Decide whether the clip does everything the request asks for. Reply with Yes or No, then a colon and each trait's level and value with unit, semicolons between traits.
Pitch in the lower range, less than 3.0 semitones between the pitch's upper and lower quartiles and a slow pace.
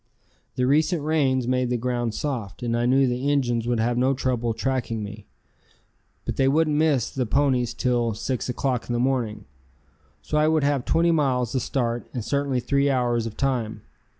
No: low, 125 Hz; narrow, 2.6 semitones; average, 185 wpm